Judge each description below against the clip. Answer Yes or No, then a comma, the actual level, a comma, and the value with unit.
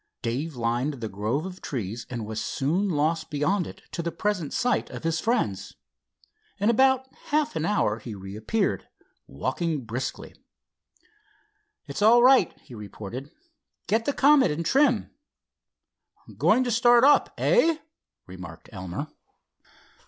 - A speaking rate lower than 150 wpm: Yes, slow, 135 wpm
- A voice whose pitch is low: No, medium, 160 Hz